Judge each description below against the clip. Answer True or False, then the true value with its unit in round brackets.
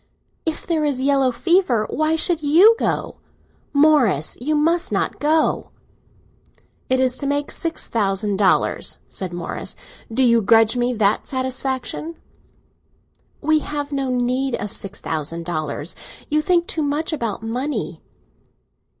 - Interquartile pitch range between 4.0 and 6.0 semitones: True (5.4 semitones)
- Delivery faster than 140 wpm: False (135 wpm)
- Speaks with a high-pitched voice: True (265 Hz)